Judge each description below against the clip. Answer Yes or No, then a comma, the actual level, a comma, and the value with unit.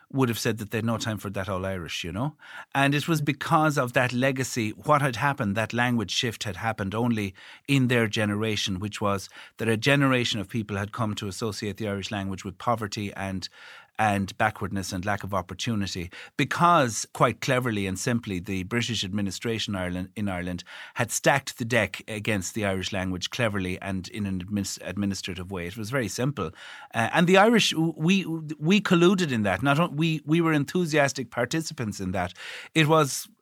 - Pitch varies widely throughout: Yes, wide, 5.8 semitones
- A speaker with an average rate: Yes, average, 190 wpm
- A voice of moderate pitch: No, low, 110 Hz